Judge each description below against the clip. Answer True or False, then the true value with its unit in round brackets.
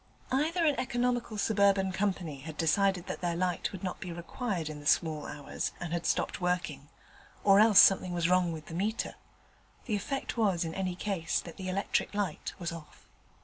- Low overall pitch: False (185 Hz)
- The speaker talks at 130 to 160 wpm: False (190 wpm)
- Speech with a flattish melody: False (3.5 semitones)